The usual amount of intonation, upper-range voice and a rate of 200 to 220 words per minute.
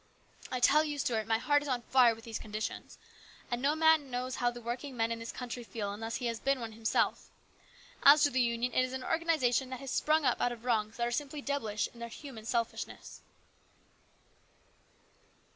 Yes: average, 3.3 semitones; high, 245 Hz; fast, 205 wpm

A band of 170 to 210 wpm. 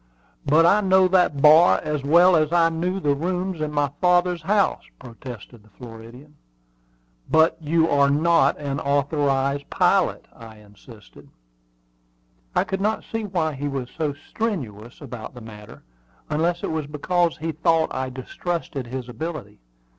No: average, 150 wpm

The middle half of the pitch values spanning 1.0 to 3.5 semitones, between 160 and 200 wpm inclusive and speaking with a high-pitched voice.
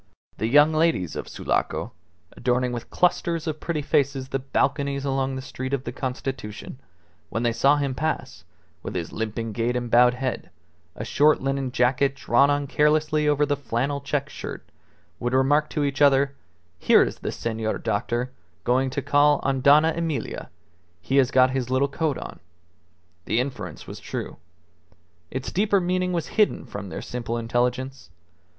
No: average, 2.9 semitones; average, 165 wpm; low, 135 Hz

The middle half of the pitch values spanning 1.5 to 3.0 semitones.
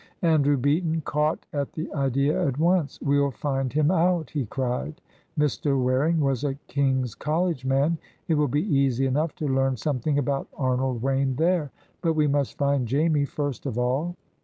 Yes: narrow, 2.6 semitones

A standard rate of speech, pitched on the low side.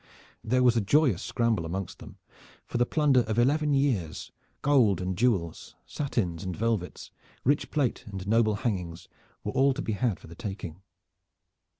Yes: average, 165 wpm; low, 115 Hz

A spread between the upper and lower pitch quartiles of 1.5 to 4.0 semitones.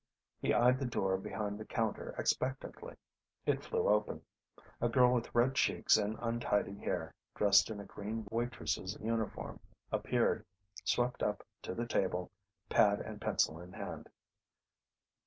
Yes: average, 2.8 semitones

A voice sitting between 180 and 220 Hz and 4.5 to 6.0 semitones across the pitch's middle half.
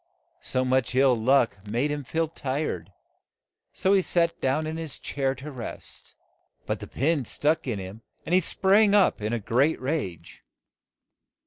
No: low, 135 Hz; average, 5.3 semitones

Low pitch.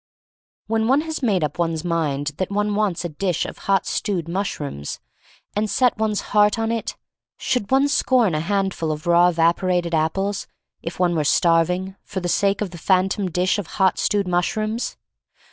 No: high, 190 Hz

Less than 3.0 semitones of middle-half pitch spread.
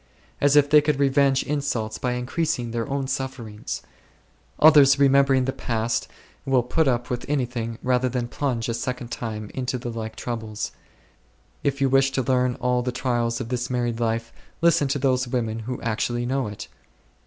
Yes: narrow, 2.6 semitones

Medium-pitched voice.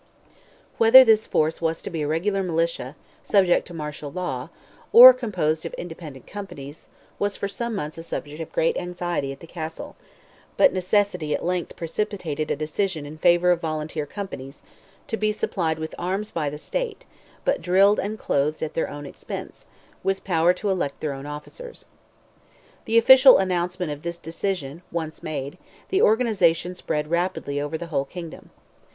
Yes: medium, 170 Hz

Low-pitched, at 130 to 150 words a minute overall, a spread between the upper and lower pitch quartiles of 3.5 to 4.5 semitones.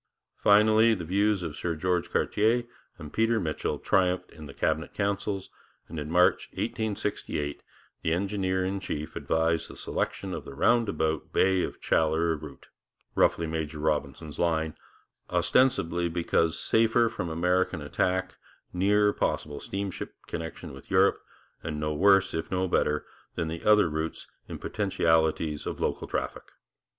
Yes: very low, 85 Hz; average, 140 wpm; average, 3.9 semitones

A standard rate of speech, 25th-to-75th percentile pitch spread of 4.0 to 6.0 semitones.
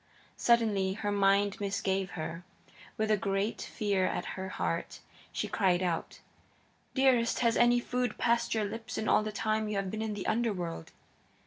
No: average, 170 wpm; average, 2.9 semitones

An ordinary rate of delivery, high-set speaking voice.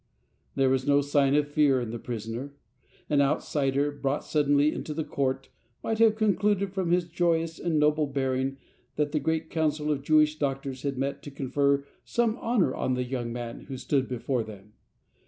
No: average, 180 wpm; medium, 145 Hz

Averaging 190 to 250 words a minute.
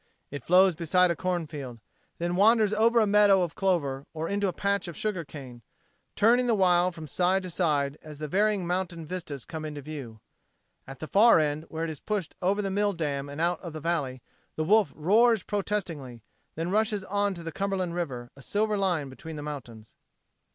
Yes: average, 200 wpm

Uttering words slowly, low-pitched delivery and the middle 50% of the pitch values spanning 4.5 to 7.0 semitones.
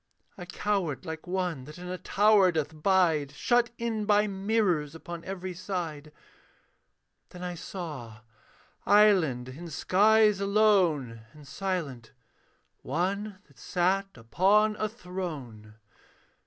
No: slow, 115 wpm; medium, 180 Hz; average, 4.8 semitones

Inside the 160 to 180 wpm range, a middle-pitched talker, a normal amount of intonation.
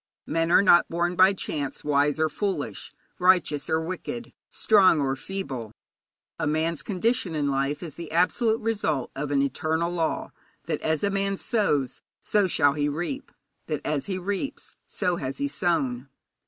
Yes: average, 165 wpm; medium, 165 Hz; average, 4.7 semitones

